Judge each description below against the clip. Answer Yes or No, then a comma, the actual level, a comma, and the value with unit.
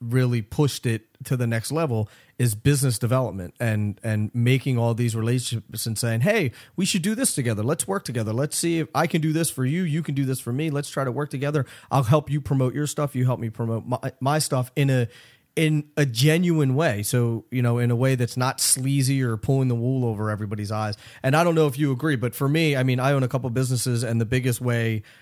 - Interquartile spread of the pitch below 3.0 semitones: No, average, 3.7 semitones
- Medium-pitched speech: No, low, 130 Hz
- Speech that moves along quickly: Yes, fast, 250 wpm